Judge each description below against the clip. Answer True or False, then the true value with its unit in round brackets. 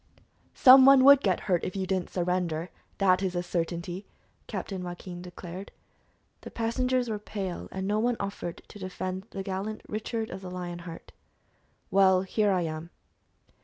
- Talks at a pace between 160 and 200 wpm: True (165 wpm)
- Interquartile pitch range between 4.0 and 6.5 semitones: False (2.9 semitones)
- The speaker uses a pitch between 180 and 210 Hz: True (190 Hz)